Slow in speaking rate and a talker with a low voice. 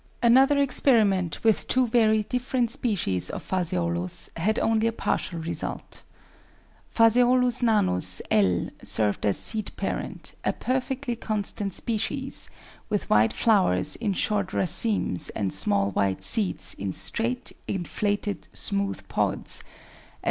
No: slow, 120 wpm; high, 210 Hz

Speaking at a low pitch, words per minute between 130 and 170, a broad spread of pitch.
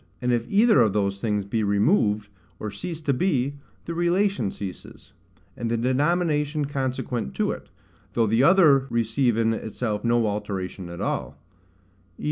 Yes: low, 120 Hz; average, 155 wpm; wide, 5.9 semitones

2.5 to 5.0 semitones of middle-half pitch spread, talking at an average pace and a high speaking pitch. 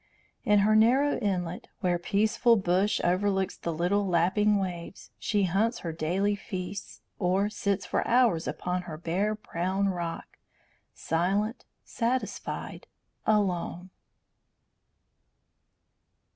No: average, 2.9 semitones; slow, 105 wpm; high, 195 Hz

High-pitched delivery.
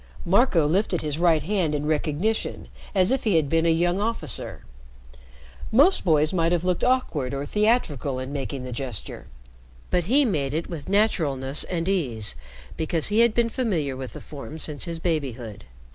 No: medium, 165 Hz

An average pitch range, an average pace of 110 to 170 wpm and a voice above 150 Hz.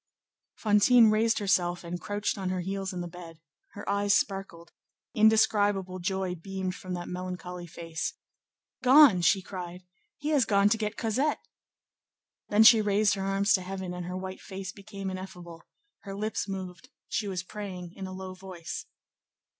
No: narrow, 2.3 semitones; average, 160 wpm; high, 190 Hz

